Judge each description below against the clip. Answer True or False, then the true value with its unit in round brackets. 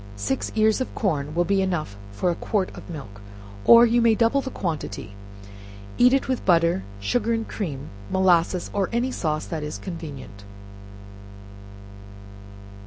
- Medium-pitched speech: True (175 Hz)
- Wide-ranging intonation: True (7.1 semitones)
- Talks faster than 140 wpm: True (150 wpm)